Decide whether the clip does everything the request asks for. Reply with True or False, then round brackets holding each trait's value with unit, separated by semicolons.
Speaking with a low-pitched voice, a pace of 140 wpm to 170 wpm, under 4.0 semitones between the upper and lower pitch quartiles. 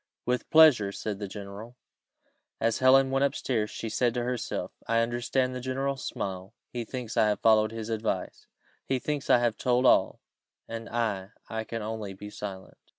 False (115 Hz; 180 wpm; 2.9 semitones)